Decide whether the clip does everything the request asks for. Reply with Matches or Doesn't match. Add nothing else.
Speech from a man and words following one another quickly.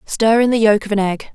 Doesn't match